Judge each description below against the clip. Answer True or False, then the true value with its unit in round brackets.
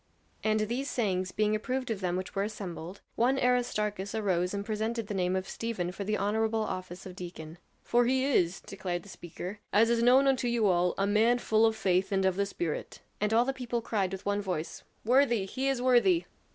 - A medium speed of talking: False (210 wpm)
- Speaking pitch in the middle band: False (210 Hz)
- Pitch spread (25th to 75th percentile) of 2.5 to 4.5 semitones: True (4.0 semitones)